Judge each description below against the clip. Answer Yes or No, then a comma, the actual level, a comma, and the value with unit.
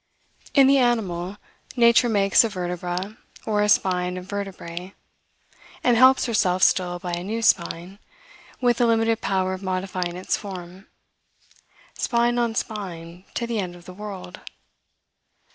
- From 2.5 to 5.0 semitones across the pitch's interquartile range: Yes, average, 4.0 semitones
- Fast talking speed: No, average, 145 wpm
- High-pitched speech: Yes, high, 195 Hz